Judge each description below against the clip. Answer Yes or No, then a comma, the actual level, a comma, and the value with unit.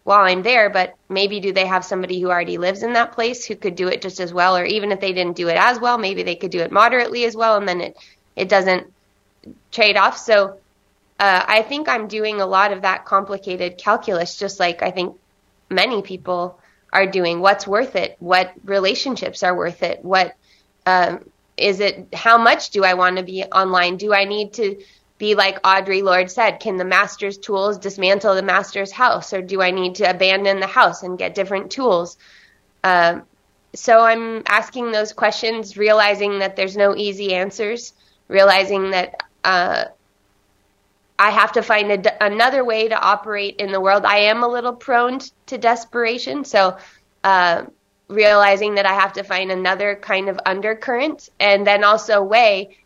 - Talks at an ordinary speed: Yes, average, 190 wpm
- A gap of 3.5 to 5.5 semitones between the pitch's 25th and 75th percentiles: No, narrow, 2.5 semitones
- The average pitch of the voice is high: Yes, high, 195 Hz